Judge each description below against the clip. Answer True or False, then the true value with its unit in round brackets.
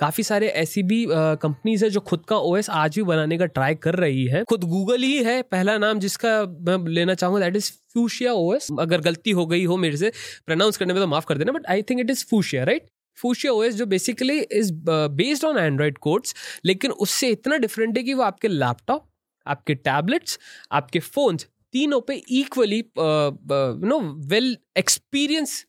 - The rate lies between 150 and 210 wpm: True (190 wpm)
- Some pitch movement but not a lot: False (6.6 semitones)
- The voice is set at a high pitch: True (195 Hz)